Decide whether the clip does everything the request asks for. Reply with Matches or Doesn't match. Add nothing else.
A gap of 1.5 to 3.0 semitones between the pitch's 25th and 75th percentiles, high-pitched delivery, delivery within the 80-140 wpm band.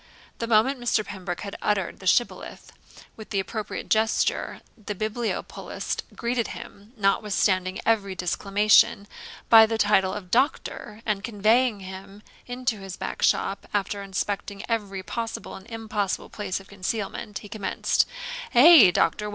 Matches